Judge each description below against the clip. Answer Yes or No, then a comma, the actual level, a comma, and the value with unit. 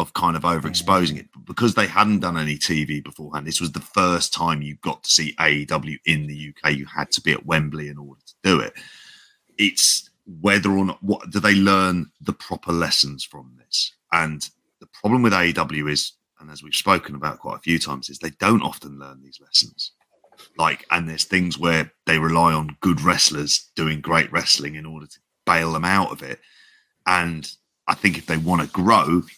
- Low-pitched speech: Yes, very low, 80 Hz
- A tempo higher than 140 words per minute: Yes, fast, 205 wpm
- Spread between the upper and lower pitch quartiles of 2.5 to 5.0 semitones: Yes, average, 2.9 semitones